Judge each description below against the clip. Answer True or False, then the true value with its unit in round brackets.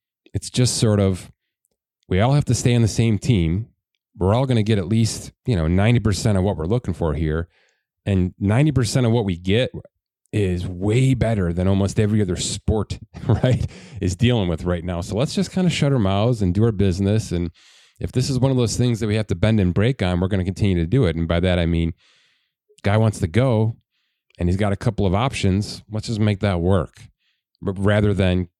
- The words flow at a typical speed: False (225 wpm)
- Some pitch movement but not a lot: True (4.0 semitones)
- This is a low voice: True (105 Hz)